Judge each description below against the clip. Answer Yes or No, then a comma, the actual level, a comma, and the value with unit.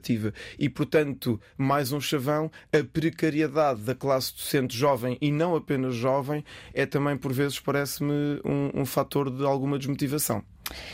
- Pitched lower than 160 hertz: Yes, medium, 140 Hz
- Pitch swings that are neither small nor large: No, narrow, 2.2 semitones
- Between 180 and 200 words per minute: No, average, 145 wpm